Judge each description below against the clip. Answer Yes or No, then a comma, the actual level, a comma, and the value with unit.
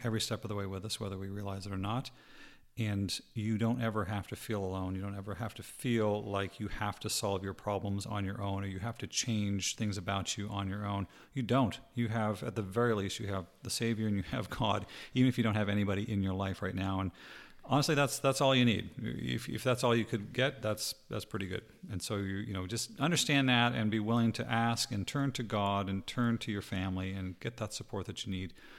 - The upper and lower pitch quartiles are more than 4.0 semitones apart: No, average, 3.0 semitones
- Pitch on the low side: Yes, low, 105 Hz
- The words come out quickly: Yes, fast, 255 wpm